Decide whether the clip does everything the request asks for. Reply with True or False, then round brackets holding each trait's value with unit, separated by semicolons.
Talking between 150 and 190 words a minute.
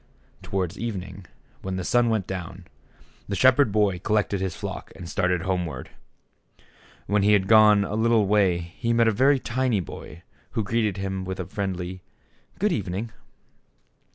True (160 wpm)